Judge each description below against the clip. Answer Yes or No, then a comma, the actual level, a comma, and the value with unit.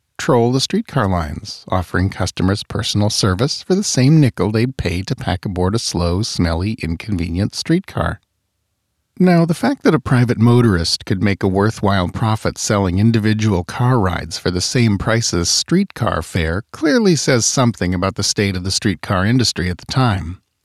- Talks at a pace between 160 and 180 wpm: Yes, average, 170 wpm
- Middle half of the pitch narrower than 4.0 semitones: No, average, 4.9 semitones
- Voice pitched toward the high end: No, low, 105 Hz